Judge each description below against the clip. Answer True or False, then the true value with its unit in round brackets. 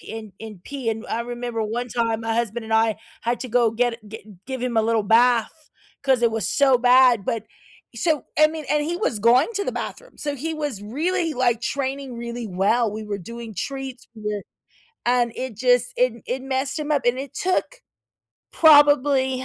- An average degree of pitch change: True (3.2 semitones)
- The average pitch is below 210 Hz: False (245 Hz)